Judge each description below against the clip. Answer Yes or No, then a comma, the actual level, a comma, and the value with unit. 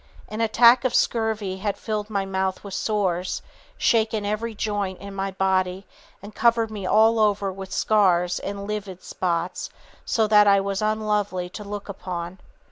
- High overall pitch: Yes, high, 200 Hz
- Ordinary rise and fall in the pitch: No, narrow, 2.2 semitones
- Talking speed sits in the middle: Yes, average, 160 wpm